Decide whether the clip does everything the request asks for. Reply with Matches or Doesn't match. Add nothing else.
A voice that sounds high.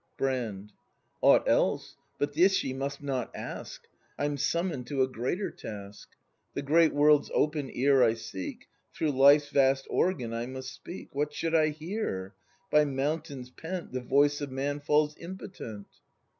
Doesn't match